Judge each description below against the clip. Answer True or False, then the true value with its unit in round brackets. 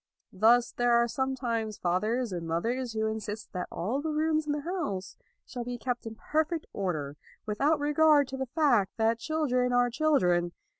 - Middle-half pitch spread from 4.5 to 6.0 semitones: True (5.4 semitones)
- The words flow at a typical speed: True (170 wpm)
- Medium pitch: False (240 Hz)